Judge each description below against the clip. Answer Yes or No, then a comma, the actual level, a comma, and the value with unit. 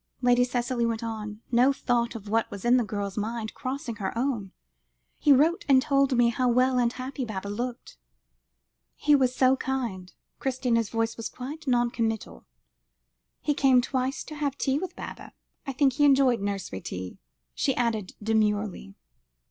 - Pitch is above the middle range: Yes, high, 245 Hz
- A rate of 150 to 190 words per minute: Yes, average, 165 wpm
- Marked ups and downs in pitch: No, average, 3.3 semitones